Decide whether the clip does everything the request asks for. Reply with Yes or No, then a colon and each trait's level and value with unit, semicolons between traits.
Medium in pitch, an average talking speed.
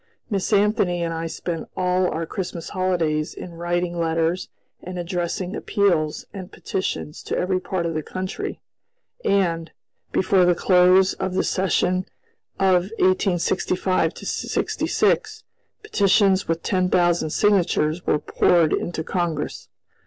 No: medium, 180 Hz; slow, 125 wpm